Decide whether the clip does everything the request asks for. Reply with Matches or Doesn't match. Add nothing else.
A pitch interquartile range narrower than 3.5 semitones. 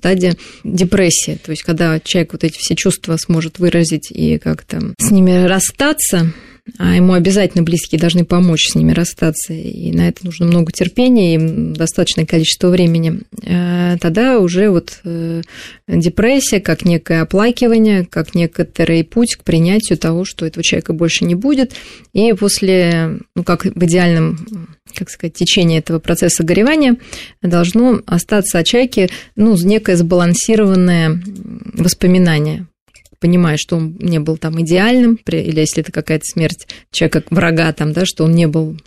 Matches